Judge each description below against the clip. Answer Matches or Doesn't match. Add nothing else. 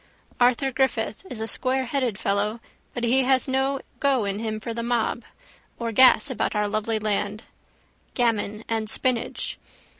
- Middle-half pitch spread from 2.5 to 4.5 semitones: Matches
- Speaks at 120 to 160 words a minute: Matches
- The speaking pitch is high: Matches